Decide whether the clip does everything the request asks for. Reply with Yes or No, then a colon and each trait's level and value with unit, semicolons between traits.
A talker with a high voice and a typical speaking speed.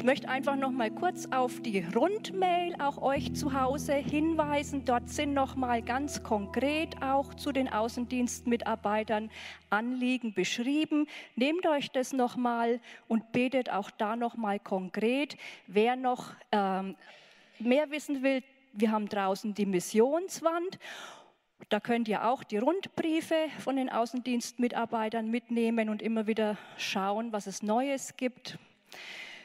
Yes: high, 245 Hz; average, 135 wpm